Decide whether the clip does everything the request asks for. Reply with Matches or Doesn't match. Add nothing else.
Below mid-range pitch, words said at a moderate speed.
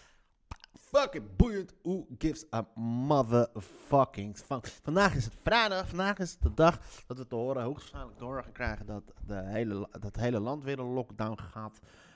Matches